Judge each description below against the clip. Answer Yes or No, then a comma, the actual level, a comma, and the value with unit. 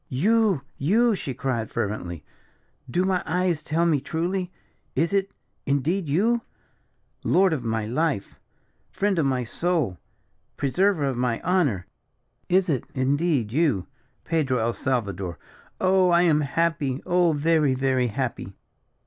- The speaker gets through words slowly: Yes, slow, 130 wpm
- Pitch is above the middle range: No, medium, 150 Hz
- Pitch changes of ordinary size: No, wide, 5.9 semitones